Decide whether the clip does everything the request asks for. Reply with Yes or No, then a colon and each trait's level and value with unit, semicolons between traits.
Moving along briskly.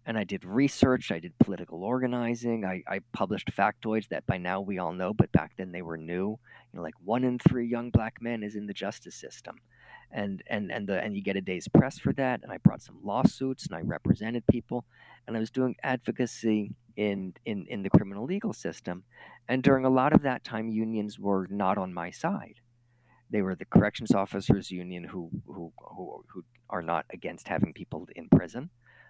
Yes: fast, 210 wpm